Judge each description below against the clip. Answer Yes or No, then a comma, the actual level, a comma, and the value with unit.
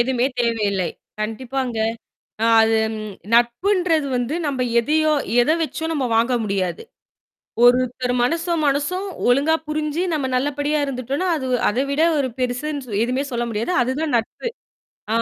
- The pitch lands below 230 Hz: No, very high, 260 Hz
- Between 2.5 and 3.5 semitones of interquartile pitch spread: No, average, 4.2 semitones